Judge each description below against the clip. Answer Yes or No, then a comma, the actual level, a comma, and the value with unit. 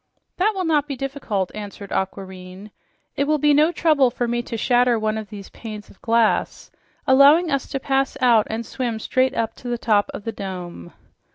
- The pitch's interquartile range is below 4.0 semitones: No, average, 4.7 semitones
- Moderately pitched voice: No, high, 235 Hz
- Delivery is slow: No, average, 195 wpm